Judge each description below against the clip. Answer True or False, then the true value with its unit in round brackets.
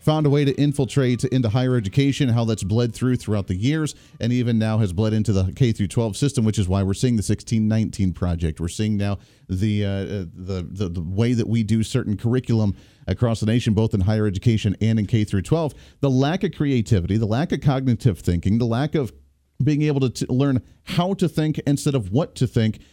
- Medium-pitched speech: False (115 Hz)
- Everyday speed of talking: False (215 wpm)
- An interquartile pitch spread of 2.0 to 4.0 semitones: False (4.7 semitones)